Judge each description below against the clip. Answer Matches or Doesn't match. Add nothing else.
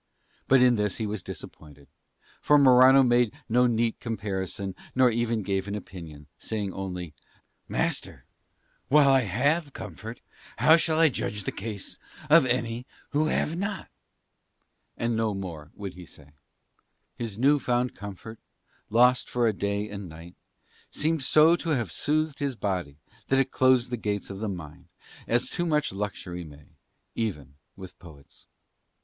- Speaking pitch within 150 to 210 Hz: Doesn't match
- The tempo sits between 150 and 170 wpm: Matches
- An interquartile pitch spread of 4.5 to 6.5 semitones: Matches